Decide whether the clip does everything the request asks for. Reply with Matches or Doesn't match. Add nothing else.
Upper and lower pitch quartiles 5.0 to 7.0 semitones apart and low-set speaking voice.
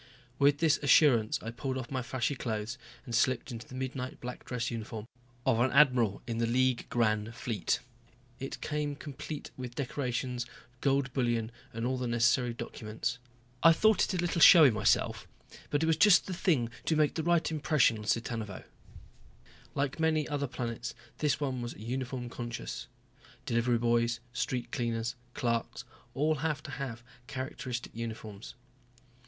Doesn't match